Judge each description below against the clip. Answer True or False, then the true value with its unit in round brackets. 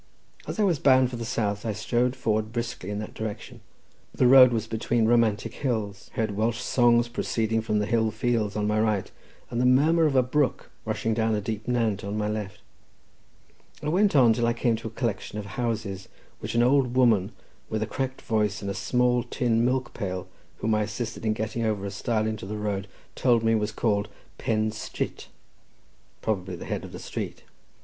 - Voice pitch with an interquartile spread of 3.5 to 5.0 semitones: False (2.4 semitones)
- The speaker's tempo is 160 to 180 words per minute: False (200 wpm)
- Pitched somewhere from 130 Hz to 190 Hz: False (110 Hz)